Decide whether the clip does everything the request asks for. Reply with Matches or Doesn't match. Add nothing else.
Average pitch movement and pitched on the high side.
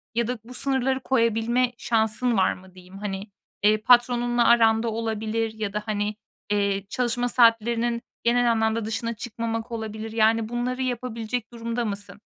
Doesn't match